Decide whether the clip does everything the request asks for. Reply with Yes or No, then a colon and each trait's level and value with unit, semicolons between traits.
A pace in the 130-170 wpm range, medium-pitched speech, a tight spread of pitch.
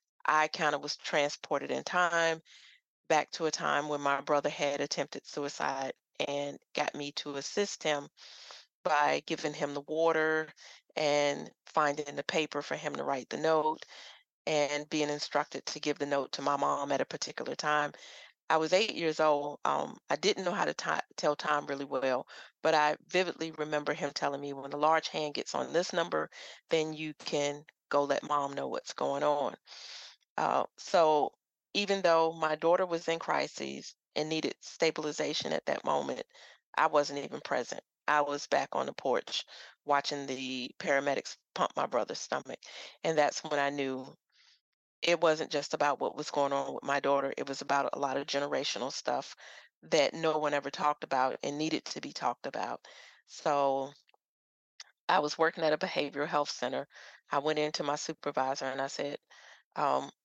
No: average, 180 wpm; medium, 150 Hz; narrow, 1.8 semitones